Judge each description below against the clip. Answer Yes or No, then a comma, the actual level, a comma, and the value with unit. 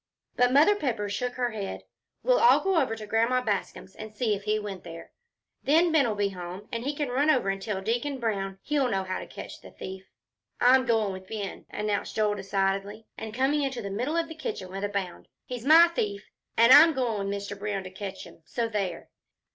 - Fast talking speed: Yes, fast, 220 wpm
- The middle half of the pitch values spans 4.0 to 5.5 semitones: Yes, average, 4.5 semitones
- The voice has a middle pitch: No, high, 215 Hz